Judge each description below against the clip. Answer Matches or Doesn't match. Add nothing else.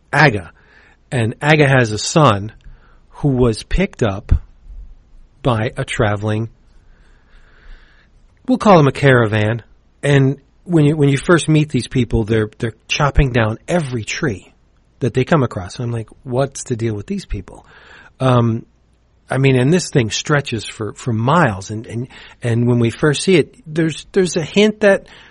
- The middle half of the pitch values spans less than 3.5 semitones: Doesn't match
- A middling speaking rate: Matches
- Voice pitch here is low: Matches